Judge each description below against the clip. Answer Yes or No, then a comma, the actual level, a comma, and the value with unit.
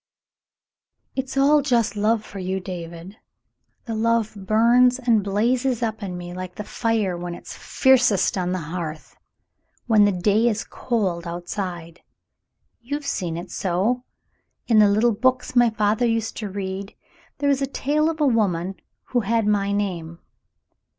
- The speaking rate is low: No, average, 155 wpm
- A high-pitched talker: Yes, high, 210 Hz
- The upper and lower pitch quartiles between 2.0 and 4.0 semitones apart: No, average, 4.5 semitones